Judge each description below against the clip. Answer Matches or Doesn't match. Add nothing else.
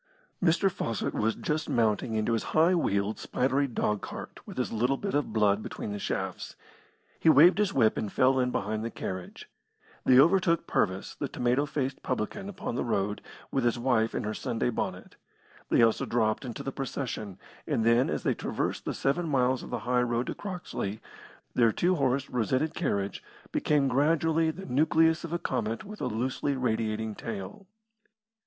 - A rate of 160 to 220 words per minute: Matches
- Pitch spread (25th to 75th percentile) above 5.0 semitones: Matches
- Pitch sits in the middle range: Doesn't match